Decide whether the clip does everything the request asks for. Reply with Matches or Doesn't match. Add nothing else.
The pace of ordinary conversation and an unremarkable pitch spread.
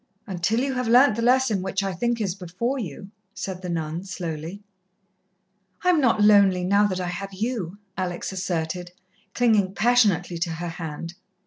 Matches